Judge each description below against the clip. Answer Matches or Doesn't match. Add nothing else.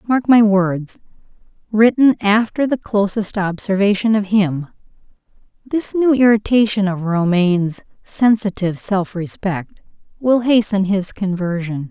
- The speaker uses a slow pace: Matches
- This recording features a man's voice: Doesn't match